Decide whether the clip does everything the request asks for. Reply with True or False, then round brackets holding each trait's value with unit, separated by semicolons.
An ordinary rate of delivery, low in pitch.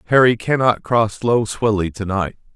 True (165 wpm; 110 Hz)